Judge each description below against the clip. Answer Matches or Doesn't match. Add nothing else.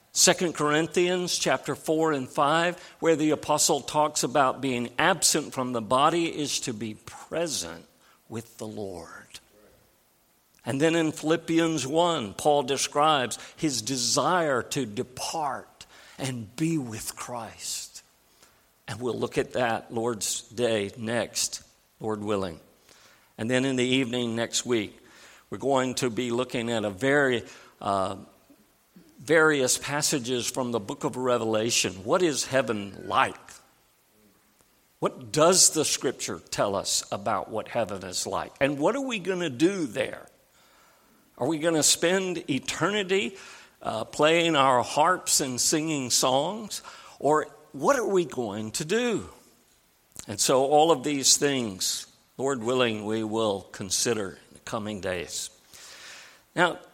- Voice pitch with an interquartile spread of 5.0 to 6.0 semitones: Matches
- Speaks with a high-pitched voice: Doesn't match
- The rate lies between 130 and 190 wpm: Matches